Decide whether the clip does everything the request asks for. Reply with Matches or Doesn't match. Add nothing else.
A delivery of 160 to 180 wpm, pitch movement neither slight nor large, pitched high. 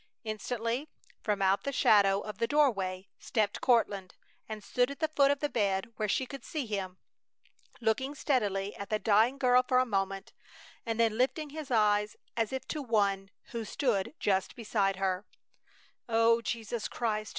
Matches